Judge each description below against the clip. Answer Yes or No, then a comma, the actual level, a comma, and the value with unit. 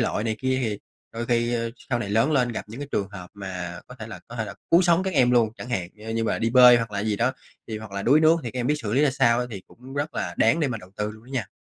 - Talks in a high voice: No, low, 115 Hz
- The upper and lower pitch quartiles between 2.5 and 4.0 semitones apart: Yes, average, 3.3 semitones